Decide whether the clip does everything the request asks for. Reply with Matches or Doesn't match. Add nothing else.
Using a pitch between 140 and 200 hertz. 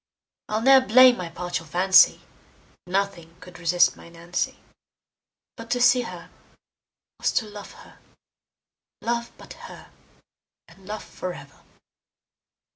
Matches